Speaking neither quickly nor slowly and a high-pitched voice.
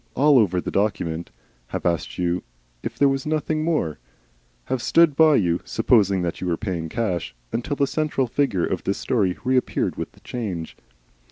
No: average, 175 wpm; low, 110 Hz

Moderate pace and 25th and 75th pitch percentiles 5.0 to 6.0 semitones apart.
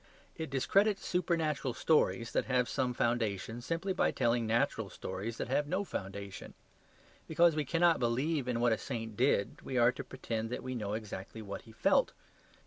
Yes: average, 175 wpm; average, 5.3 semitones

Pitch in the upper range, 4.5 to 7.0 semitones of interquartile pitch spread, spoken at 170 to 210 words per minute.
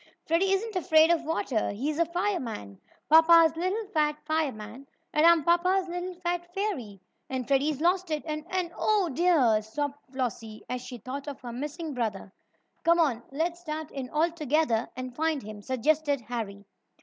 No: very high, 305 Hz; average, 5.3 semitones; average, 160 wpm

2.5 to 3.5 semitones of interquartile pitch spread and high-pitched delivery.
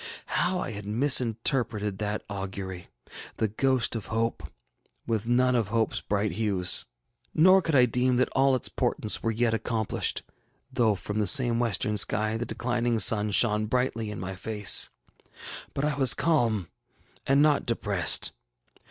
No: average, 3.2 semitones; low, 115 Hz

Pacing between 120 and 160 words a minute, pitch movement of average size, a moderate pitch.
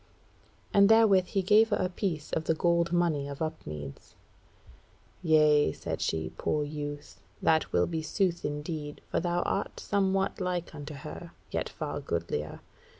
Yes: average, 150 wpm; average, 3.8 semitones; medium, 160 Hz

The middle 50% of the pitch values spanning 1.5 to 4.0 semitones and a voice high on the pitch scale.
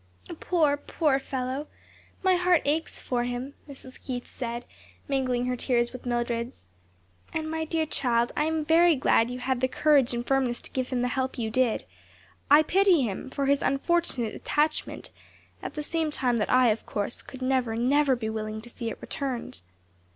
Yes: average, 3.6 semitones; very high, 260 Hz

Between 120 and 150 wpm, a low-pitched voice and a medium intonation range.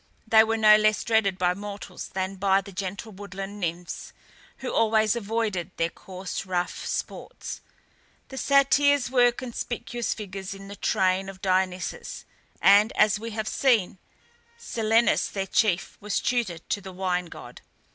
No: average, 145 wpm; high, 200 Hz; average, 3.0 semitones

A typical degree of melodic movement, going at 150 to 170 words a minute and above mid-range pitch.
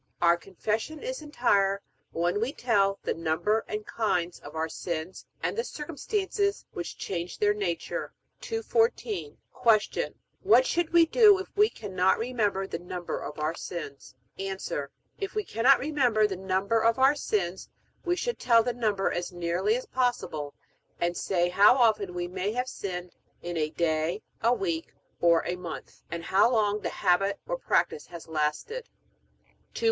No: wide, 6.8 semitones; average, 160 wpm; high, 205 Hz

